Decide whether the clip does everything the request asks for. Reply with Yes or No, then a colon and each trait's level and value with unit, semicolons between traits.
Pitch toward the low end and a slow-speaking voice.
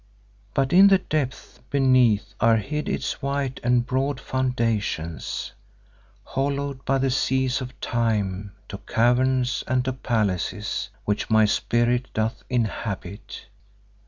Yes: low, 125 Hz; slow, 120 wpm